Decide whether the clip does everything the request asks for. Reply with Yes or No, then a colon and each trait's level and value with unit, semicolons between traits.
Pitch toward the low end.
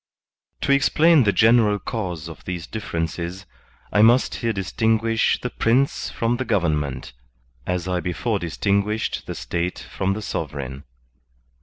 Yes: low, 100 Hz